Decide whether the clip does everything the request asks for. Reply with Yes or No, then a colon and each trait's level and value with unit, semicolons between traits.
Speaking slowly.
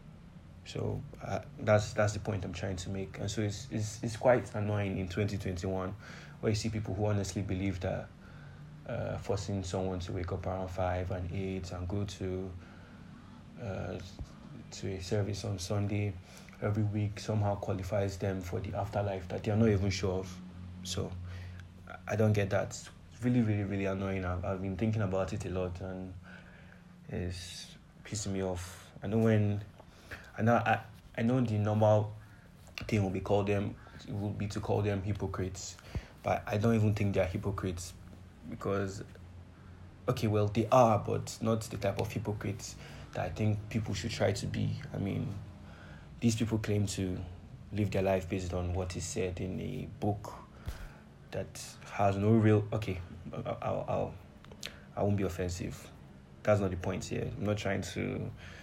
No: average, 170 wpm